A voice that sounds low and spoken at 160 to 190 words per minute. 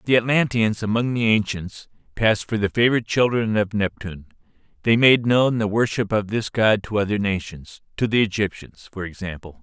Yes: low, 105 Hz; average, 170 wpm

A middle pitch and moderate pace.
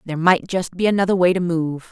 No: medium, 175 Hz; fast, 250 wpm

